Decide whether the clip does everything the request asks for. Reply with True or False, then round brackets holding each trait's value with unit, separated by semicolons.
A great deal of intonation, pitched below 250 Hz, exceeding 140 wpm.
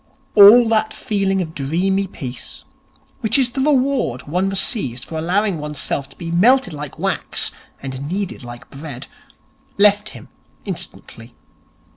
False (6.5 semitones; 190 Hz; 135 wpm)